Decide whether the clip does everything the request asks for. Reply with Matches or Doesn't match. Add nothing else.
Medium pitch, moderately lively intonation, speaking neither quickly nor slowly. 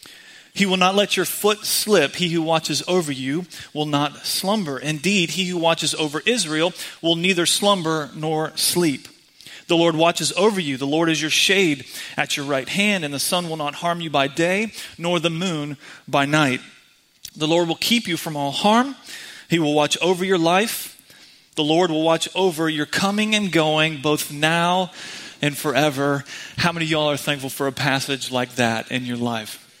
Matches